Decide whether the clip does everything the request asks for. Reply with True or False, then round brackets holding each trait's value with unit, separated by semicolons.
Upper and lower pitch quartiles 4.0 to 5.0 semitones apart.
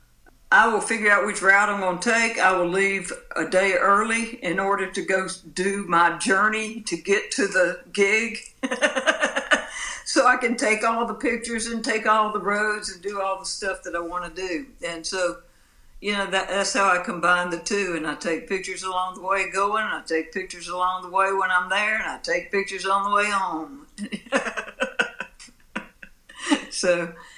False (3.6 semitones)